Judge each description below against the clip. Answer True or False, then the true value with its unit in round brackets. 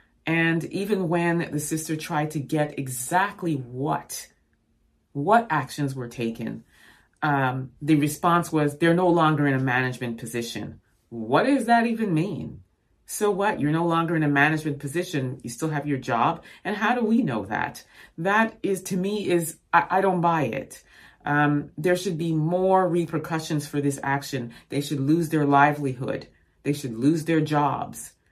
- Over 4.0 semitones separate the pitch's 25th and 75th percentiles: False (3.6 semitones)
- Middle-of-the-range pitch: True (155 Hz)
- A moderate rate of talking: True (165 wpm)